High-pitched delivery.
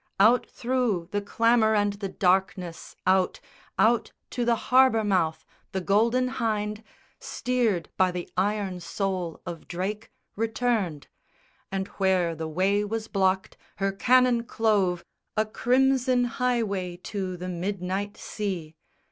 Yes: high, 205 Hz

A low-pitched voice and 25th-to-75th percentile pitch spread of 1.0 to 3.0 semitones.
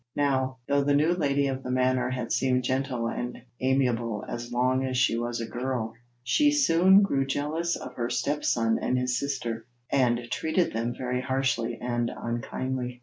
Yes: low, 130 Hz; narrow, 2.6 semitones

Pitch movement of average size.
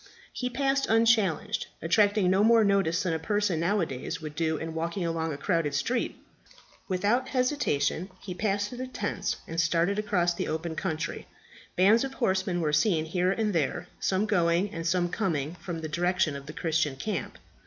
Yes: average, 4.3 semitones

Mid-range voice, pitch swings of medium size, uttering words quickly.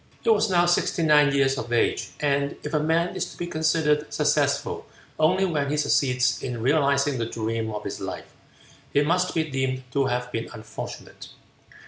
No: medium, 145 Hz; average, 3.5 semitones; average, 180 wpm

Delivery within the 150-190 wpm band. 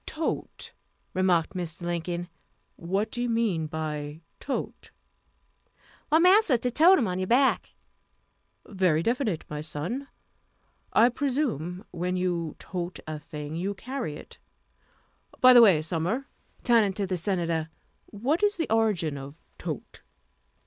No: slow, 135 wpm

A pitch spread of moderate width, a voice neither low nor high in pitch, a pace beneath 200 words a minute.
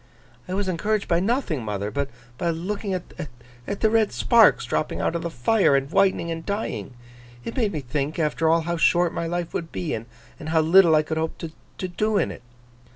No: average, 4.0 semitones; medium, 170 Hz; fast, 205 wpm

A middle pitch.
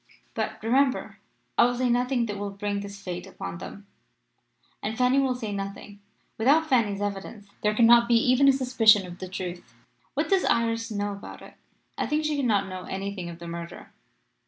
No: high, 215 Hz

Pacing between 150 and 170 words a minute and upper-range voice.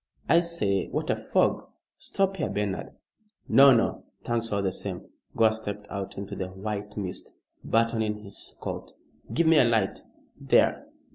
No: average, 155 wpm; low, 105 Hz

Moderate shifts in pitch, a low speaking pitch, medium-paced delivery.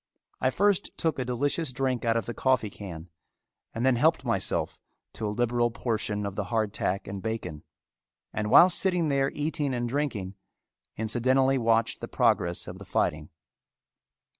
Yes: average, 4.4 semitones; low, 120 Hz; average, 165 wpm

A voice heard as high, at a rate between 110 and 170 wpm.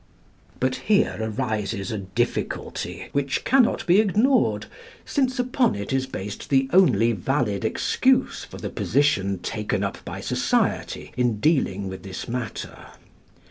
No: low, 125 Hz; slow, 135 wpm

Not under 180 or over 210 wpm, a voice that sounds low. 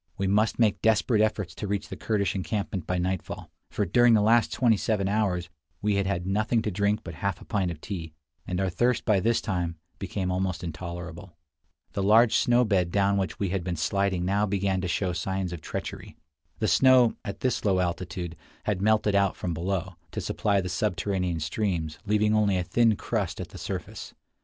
Yes: average, 200 wpm; very low, 95 Hz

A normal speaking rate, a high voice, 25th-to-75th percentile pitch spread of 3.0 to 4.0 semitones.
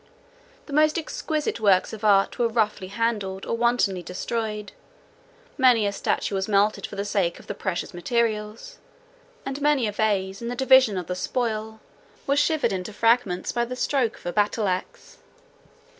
Yes: average, 170 wpm; high, 215 Hz; average, 3.6 semitones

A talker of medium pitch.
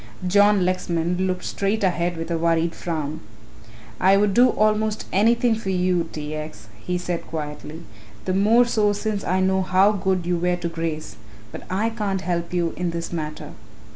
Yes: medium, 180 Hz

